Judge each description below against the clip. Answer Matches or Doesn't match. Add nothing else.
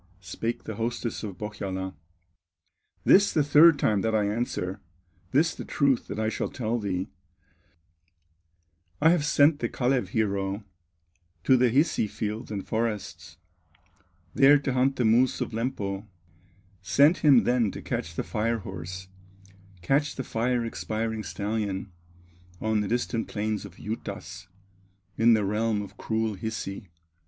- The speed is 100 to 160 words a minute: Matches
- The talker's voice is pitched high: Doesn't match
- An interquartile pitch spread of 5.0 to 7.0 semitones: Doesn't match